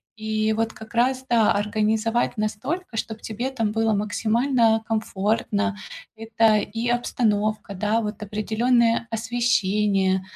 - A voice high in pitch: Yes, high, 220 Hz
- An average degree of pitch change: No, narrow, 1.6 semitones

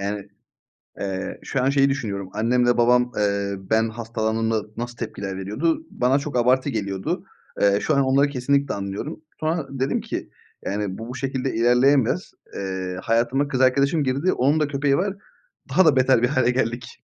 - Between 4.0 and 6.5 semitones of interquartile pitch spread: Yes, average, 4.3 semitones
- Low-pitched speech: Yes, low, 125 Hz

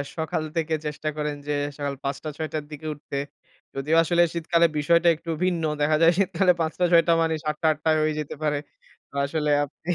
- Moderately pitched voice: Yes, medium, 155 Hz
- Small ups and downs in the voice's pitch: Yes, narrow, 1.9 semitones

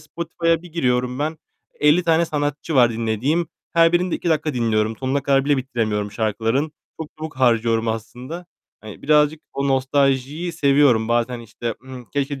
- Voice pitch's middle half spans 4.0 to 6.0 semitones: Yes, average, 4.7 semitones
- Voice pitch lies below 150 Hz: Yes, low, 135 Hz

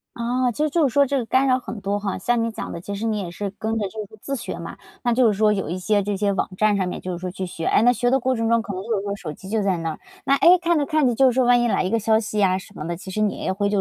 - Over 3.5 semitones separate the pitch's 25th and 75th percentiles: Yes, average, 3.9 semitones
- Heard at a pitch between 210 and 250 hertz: Yes, high, 215 Hz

